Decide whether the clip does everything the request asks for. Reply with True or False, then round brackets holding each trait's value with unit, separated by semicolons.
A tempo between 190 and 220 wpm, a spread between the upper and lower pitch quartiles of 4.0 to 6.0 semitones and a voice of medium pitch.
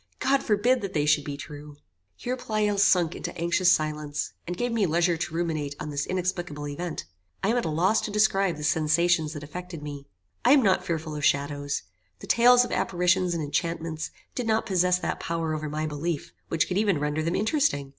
True (205 wpm; 4.3 semitones; 170 Hz)